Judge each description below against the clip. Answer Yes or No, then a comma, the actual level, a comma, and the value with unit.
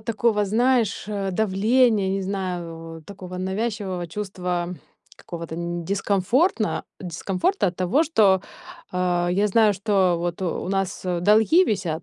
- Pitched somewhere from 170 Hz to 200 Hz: Yes, high, 190 Hz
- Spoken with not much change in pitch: No, average, 3.1 semitones